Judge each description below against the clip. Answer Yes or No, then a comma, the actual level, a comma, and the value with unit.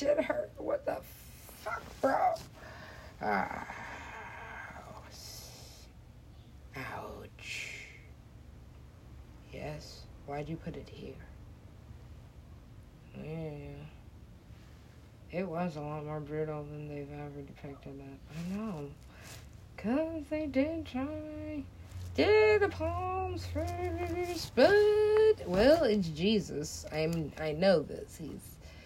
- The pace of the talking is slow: Yes, slow, 95 wpm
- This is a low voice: No, medium, 155 Hz